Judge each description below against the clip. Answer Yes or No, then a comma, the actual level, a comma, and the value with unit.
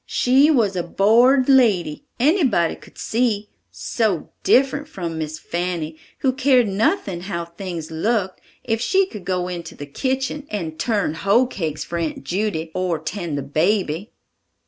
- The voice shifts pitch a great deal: Yes, wide, 6.6 semitones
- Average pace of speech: Yes, average, 150 wpm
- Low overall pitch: No, high, 195 Hz